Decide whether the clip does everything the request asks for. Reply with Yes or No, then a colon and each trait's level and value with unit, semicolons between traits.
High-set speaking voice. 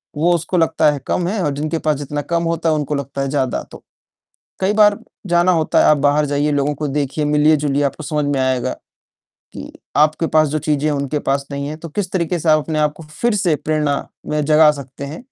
No: medium, 150 Hz